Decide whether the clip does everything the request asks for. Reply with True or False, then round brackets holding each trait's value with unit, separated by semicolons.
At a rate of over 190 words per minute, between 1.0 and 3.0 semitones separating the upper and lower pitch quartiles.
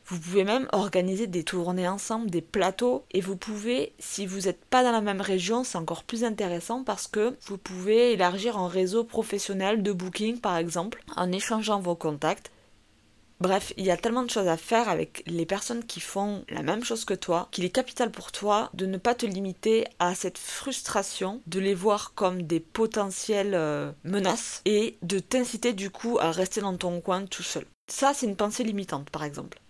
False (200 wpm; 3.9 semitones)